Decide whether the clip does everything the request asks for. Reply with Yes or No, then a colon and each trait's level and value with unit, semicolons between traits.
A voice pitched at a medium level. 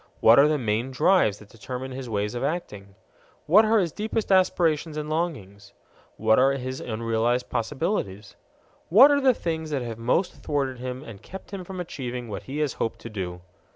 No: low, 130 Hz